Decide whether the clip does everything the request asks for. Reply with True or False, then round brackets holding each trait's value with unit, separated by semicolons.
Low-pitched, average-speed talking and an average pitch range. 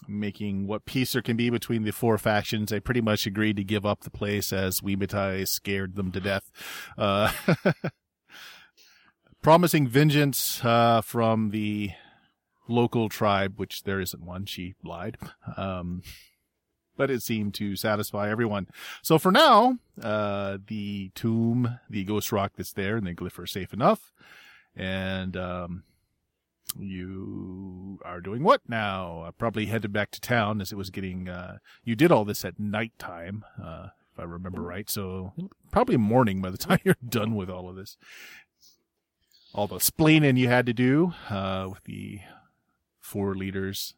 True (105 Hz; 160 wpm; 3.4 semitones)